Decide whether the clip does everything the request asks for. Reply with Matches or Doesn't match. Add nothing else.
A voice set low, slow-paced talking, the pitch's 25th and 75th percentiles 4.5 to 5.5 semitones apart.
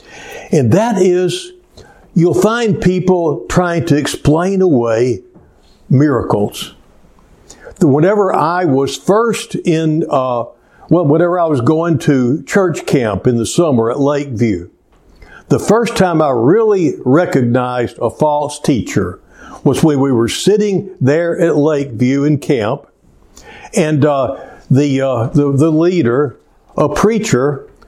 Doesn't match